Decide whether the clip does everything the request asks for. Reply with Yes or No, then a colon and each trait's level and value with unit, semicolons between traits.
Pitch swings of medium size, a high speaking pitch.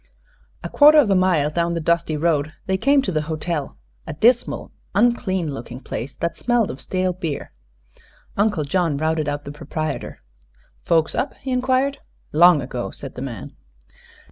No: average, 4.9 semitones; medium, 170 Hz